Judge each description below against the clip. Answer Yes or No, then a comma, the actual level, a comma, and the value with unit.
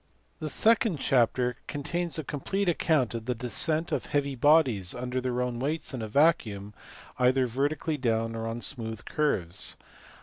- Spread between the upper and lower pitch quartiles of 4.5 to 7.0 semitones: Yes, average, 4.9 semitones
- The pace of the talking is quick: No, average, 160 wpm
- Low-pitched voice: Yes, low, 130 Hz